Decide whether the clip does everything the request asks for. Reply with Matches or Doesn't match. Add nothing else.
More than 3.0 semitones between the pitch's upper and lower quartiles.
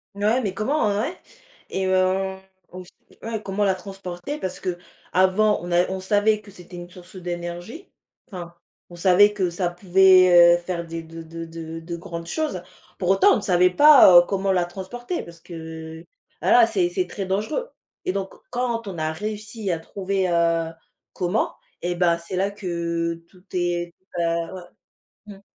Doesn't match